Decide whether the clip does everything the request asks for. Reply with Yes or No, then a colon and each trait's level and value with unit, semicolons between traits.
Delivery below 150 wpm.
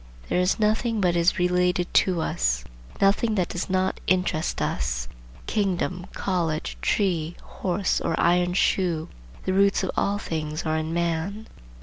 Yes: slow, 135 wpm